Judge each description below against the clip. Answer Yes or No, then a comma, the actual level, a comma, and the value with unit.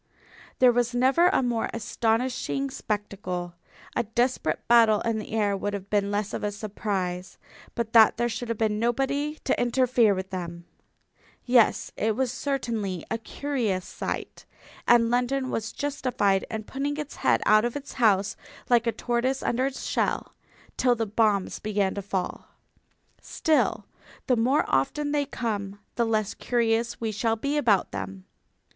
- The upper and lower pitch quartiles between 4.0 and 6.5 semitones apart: No, average, 3.5 semitones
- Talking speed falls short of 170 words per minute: Yes, average, 160 wpm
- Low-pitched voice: No, high, 225 Hz